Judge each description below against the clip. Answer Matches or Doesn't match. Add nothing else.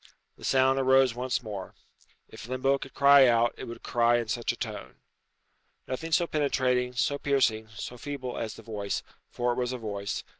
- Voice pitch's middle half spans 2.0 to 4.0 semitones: Matches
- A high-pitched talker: Doesn't match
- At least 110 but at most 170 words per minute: Doesn't match